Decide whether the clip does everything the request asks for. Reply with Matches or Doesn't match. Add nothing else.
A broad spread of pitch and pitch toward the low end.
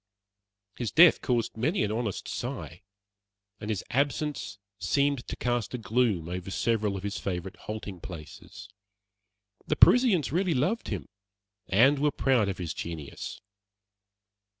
Matches